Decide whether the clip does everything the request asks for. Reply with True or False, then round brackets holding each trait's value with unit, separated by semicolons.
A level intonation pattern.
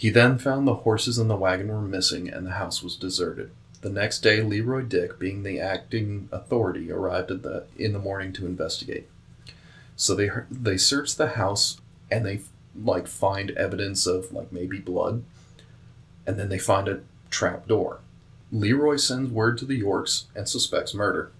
False (4.2 semitones)